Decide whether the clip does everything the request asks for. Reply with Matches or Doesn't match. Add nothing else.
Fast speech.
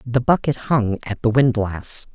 Doesn't match